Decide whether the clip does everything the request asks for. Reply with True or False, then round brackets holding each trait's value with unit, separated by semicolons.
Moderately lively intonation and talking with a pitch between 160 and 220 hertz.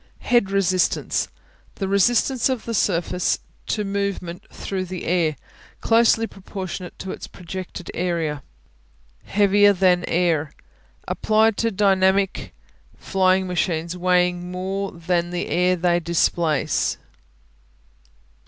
False (2.2 semitones; 185 Hz)